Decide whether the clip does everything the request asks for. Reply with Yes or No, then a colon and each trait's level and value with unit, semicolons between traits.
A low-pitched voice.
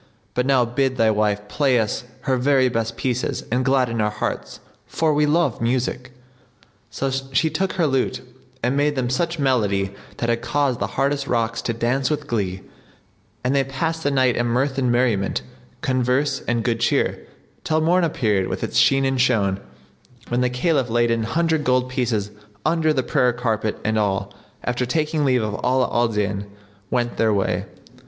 Yes: low, 125 Hz